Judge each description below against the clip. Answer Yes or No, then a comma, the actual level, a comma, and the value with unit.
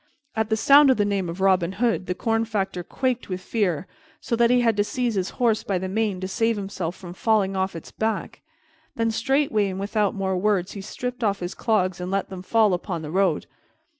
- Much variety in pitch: No, average, 3.2 semitones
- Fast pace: Yes, fast, 225 wpm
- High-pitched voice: Yes, high, 200 Hz